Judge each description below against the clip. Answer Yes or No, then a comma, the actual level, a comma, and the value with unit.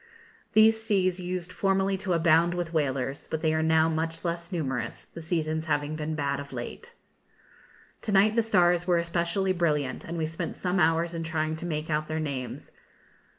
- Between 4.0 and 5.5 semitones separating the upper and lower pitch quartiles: No, narrow, 2.4 semitones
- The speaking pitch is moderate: Yes, medium, 165 Hz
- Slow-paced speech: No, average, 185 wpm